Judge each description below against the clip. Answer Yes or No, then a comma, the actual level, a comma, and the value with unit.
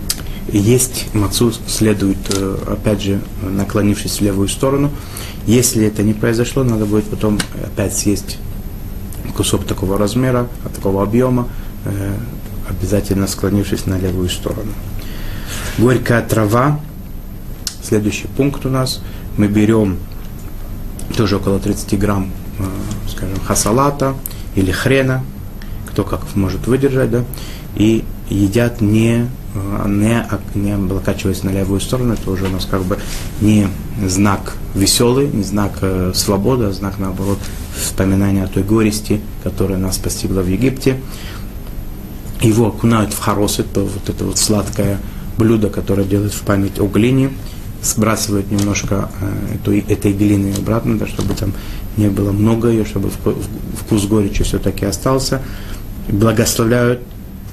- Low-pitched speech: Yes, low, 100 Hz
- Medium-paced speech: Yes, average, 125 wpm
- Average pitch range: No, narrow, 2.0 semitones